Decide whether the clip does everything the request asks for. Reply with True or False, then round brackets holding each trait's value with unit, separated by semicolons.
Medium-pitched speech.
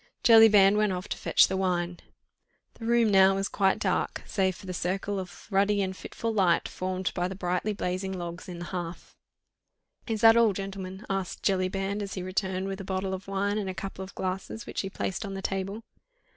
False (195 Hz)